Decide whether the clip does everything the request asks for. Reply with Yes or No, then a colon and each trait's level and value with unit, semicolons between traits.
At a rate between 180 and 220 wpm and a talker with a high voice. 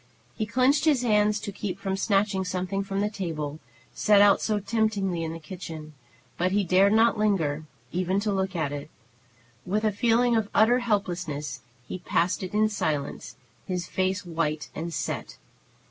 No: average, 170 wpm; high, 195 Hz